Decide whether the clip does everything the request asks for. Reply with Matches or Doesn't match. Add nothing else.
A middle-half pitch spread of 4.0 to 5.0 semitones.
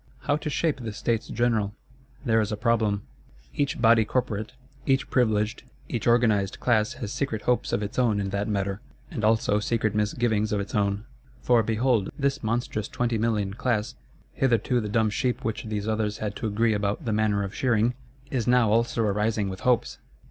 Doesn't match